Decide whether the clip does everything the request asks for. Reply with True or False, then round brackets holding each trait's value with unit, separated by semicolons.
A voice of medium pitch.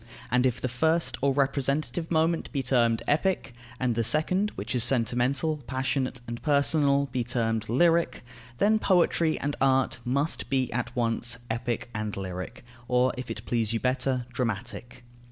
False (130 Hz)